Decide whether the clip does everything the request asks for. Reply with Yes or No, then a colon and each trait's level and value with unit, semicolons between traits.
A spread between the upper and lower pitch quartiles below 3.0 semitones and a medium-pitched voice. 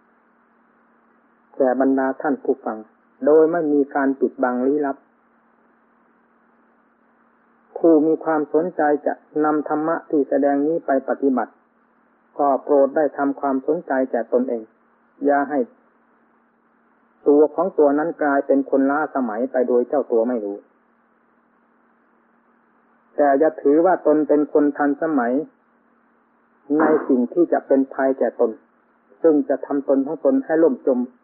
Yes: narrow, 2.4 semitones; medium, 145 Hz